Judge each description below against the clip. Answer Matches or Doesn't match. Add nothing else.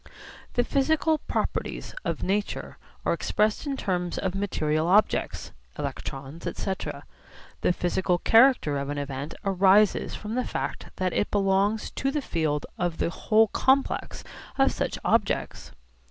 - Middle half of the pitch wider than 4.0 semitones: Matches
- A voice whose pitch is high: Matches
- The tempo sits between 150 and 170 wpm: Doesn't match